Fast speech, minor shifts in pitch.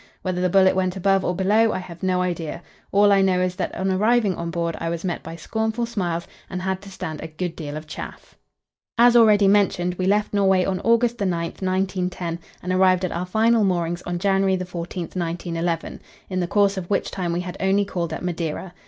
Yes: fast, 215 wpm; narrow, 2.2 semitones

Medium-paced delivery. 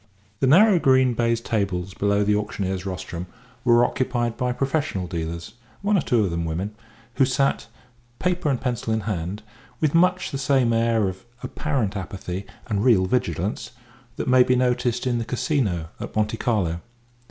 Yes: average, 165 wpm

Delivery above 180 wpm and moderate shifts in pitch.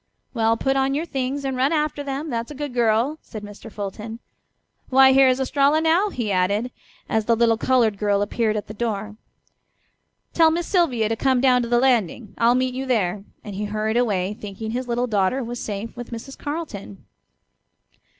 Yes: average, 190 wpm; average, 4.0 semitones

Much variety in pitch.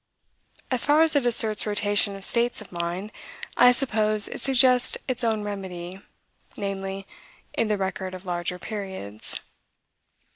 No: average, 3.8 semitones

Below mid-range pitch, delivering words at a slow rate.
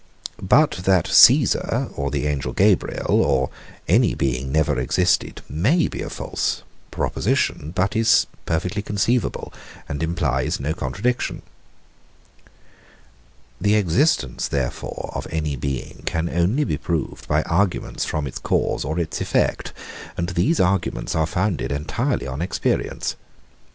Yes: very low, 80 Hz; slow, 130 wpm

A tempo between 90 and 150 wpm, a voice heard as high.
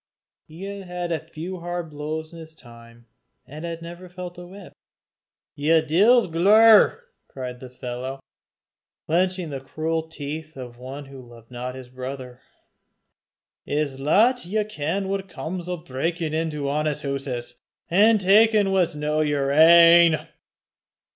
No: average, 140 wpm; medium, 160 Hz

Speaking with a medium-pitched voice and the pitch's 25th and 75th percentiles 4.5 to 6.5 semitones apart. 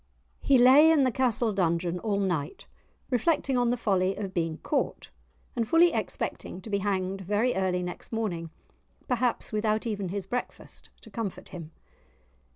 No: high, 210 Hz; average, 4.8 semitones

